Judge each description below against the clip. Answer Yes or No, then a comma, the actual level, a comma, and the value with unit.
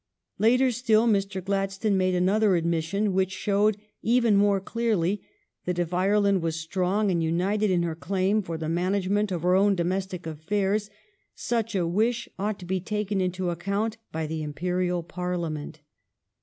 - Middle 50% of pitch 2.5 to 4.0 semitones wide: Yes, average, 2.9 semitones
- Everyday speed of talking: Yes, average, 160 wpm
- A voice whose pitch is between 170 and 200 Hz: Yes, high, 190 Hz